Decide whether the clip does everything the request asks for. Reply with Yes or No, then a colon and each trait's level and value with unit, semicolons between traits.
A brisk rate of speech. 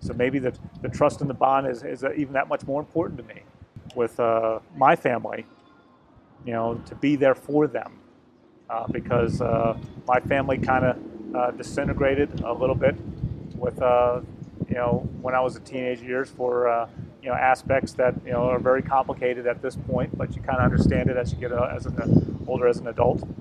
Yes: fast, 210 wpm